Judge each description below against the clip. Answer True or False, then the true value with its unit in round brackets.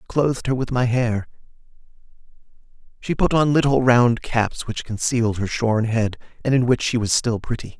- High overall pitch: False (120 Hz)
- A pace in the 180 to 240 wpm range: True (190 wpm)